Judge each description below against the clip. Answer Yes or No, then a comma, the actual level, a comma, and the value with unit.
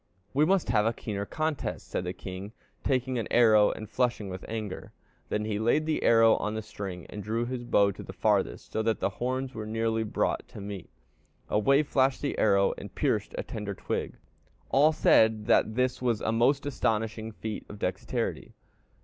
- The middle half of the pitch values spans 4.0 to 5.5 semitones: No, average, 3.3 semitones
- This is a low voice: Yes, low, 110 Hz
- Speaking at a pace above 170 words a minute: Yes, average, 190 wpm